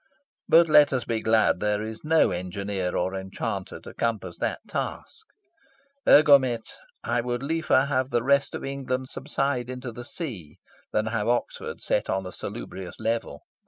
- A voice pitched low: Yes, low, 120 Hz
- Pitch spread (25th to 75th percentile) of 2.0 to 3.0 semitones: No, average, 4.7 semitones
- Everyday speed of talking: Yes, average, 160 wpm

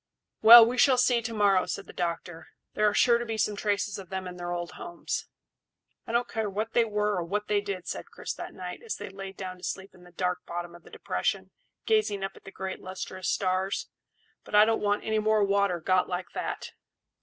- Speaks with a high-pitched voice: Yes, high, 200 Hz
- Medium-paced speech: No, fast, 230 wpm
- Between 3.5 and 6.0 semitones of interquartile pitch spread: No, average, 2.9 semitones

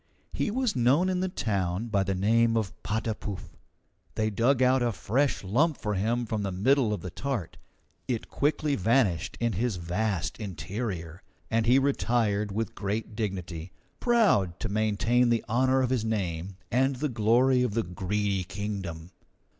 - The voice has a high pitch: No, low, 110 Hz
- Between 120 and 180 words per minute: Yes, average, 160 wpm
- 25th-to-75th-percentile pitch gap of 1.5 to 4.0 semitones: No, average, 4.4 semitones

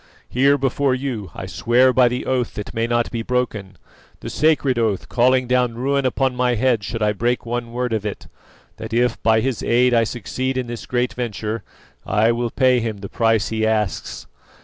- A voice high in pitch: No, low, 120 Hz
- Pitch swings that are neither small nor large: No, narrow, 2.1 semitones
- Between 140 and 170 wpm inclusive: No, average, 195 wpm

